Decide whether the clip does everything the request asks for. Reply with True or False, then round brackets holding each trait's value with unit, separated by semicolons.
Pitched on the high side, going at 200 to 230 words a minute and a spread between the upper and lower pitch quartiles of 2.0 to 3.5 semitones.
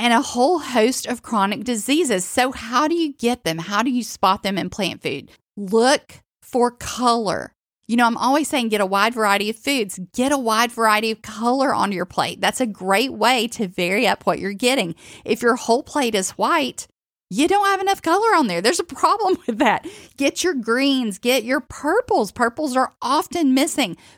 False (245 Hz; 205 wpm; 4.8 semitones)